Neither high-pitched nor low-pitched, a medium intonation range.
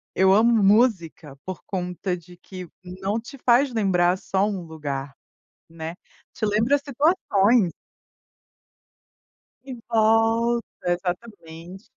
No: high, 195 Hz; average, 4.6 semitones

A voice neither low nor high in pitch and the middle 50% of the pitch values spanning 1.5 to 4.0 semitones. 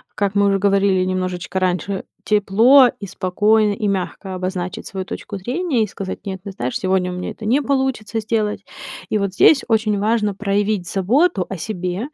No: high, 200 Hz; average, 2.7 semitones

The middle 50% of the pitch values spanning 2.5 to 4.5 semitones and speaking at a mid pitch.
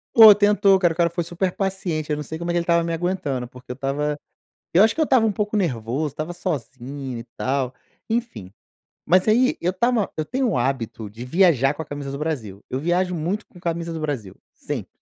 No: wide, 5.6 semitones; medium, 165 Hz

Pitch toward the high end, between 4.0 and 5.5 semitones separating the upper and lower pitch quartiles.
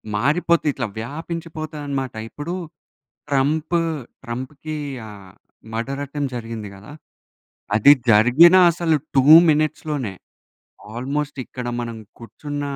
No: medium, 140 Hz; average, 4.6 semitones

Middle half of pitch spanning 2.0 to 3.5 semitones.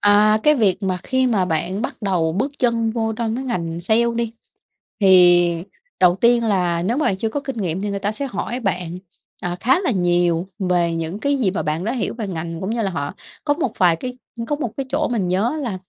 No: average, 5.1 semitones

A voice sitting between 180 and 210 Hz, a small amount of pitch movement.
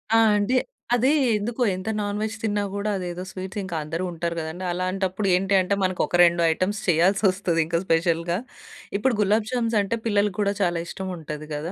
No: medium, 185 Hz; average, 3.1 semitones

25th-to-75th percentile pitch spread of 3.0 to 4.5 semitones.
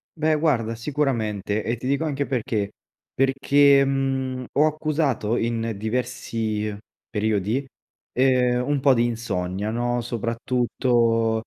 Yes: average, 3.4 semitones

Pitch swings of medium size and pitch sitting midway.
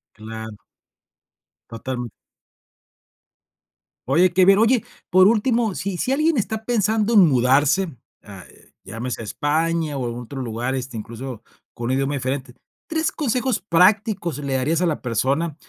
No: wide, 8.3 semitones; medium, 150 Hz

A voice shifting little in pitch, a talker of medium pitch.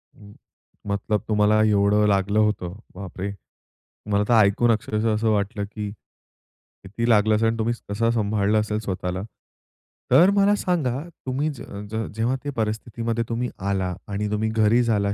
No: narrow, 2.3 semitones; low, 110 Hz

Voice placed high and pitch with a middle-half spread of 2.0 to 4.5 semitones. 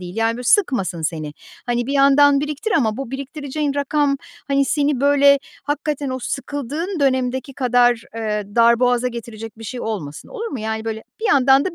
Yes: very high, 260 Hz; average, 4.0 semitones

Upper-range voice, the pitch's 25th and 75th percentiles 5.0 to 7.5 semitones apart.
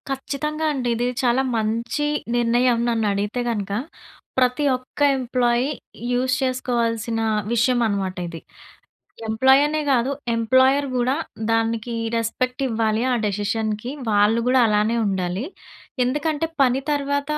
No: high, 240 Hz; average, 2.7 semitones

